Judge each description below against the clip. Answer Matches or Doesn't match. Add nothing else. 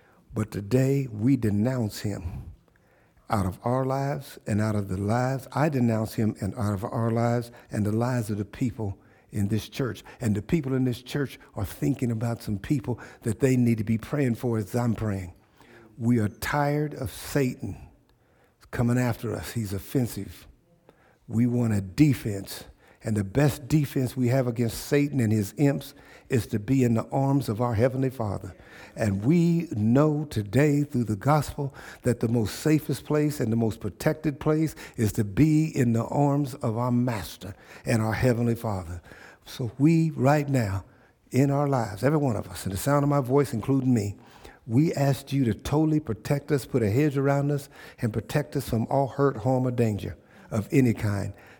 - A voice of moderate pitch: Doesn't match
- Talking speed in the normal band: Matches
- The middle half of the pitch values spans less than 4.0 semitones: Doesn't match